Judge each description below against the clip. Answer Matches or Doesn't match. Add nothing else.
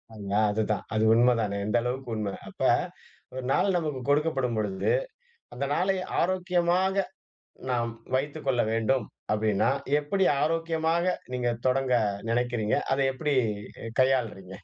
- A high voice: Doesn't match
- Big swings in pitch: Matches